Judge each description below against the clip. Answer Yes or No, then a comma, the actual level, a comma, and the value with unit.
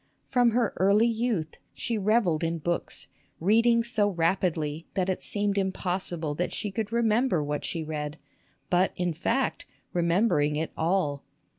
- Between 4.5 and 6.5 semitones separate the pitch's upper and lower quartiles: Yes, average, 5.1 semitones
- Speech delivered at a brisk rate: No, average, 145 wpm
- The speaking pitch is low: No, medium, 185 Hz